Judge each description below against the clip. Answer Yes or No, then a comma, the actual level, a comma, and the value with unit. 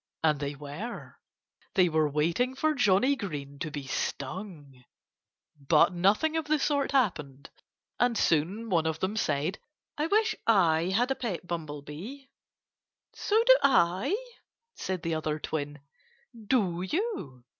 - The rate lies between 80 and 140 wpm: Yes, slow, 135 wpm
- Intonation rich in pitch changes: Yes, wide, 8.5 semitones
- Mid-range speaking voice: Yes, medium, 180 Hz